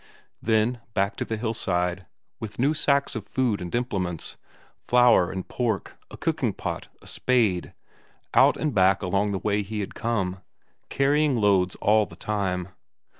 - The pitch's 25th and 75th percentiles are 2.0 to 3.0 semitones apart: No, average, 4.2 semitones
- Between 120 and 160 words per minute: Yes, average, 155 wpm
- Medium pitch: No, low, 105 Hz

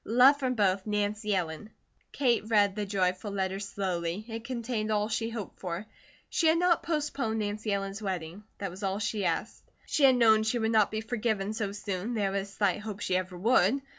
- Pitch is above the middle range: Yes, high, 210 Hz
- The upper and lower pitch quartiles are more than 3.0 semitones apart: No, narrow, 2.6 semitones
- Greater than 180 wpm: Yes, average, 195 wpm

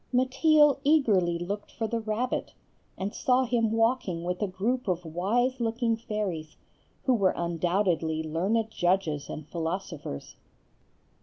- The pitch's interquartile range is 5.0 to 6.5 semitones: Yes, wide, 5.6 semitones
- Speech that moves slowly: Yes, slow, 130 wpm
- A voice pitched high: Yes, high, 205 Hz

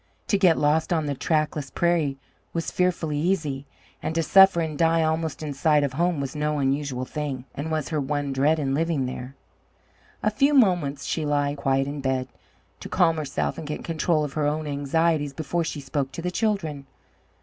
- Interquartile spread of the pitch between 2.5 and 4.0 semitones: Yes, average, 2.8 semitones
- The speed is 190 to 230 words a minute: Yes, average, 195 wpm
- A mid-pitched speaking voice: Yes, medium, 150 Hz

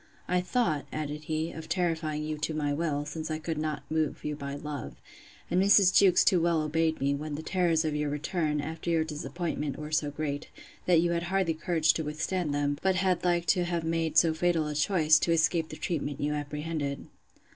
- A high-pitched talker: No, medium, 155 Hz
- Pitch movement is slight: Yes, narrow, 2.3 semitones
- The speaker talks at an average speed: No, fast, 210 wpm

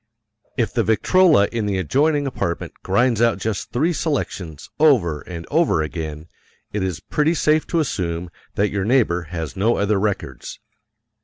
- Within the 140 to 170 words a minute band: Yes, average, 155 wpm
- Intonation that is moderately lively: No, wide, 7.8 semitones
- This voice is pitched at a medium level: No, low, 105 Hz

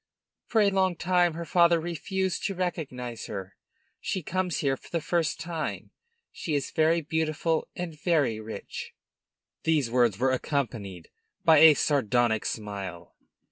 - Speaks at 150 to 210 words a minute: No, average, 140 wpm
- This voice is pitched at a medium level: Yes, medium, 155 Hz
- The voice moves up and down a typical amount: No, wide, 6.0 semitones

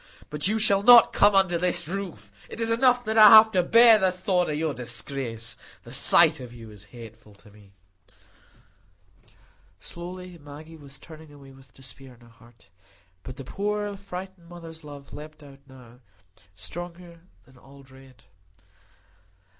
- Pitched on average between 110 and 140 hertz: No, medium, 155 Hz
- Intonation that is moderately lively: No, wide, 6.7 semitones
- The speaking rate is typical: Yes, average, 160 wpm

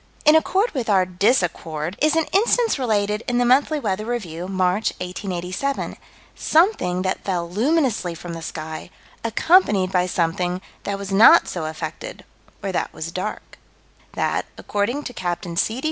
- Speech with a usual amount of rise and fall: No, wide, 6.0 semitones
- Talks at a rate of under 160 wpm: Yes, average, 150 wpm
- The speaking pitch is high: Yes, high, 200 Hz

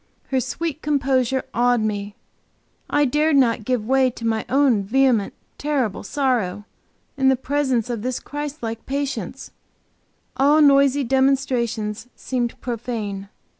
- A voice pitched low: No, very high, 255 Hz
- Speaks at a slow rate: Yes, slow, 130 wpm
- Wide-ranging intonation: No, average, 3.4 semitones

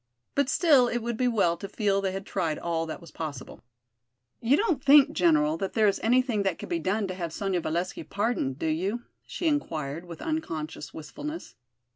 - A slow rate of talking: No, average, 195 wpm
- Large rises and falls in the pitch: Yes, wide, 7.0 semitones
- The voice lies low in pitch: No, high, 195 Hz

